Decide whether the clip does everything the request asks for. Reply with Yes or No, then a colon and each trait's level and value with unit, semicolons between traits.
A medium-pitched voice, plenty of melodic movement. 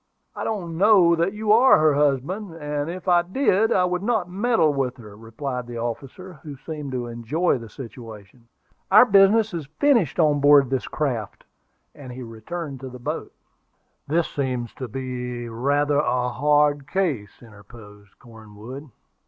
Yes: medium, 145 Hz; wide, 6.3 semitones